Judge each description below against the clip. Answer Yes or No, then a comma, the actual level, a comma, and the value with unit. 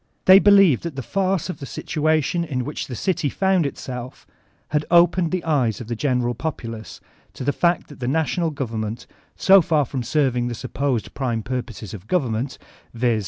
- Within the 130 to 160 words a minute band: No, average, 185 wpm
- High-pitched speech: No, medium, 140 Hz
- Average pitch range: No, wide, 5.7 semitones